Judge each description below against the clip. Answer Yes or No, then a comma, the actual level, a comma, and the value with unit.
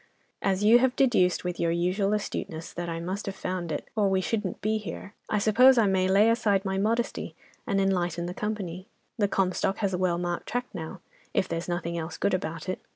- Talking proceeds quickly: Yes, fast, 215 wpm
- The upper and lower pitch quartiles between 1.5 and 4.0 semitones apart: Yes, average, 3.1 semitones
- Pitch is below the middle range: No, high, 190 Hz